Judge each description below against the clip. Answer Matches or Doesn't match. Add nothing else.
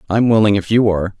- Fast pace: Matches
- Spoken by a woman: Doesn't match